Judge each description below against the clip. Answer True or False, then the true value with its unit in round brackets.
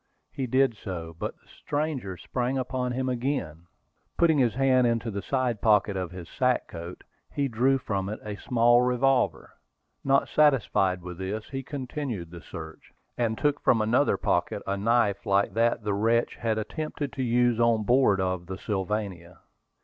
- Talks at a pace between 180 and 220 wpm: False (170 wpm)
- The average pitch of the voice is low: True (115 Hz)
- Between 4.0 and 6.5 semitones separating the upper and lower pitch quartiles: True (4.8 semitones)